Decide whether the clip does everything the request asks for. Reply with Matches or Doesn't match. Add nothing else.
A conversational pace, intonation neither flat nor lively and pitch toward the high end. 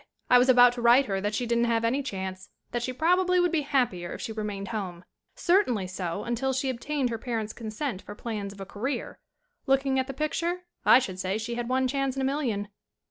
Doesn't match